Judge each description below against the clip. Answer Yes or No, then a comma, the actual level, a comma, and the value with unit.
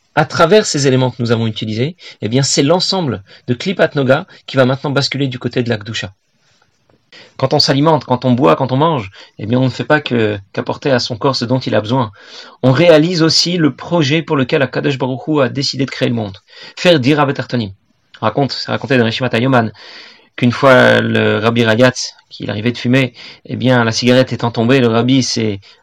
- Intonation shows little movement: No, average, 3.3 semitones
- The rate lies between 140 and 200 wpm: No, average, 210 wpm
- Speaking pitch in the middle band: No, low, 130 Hz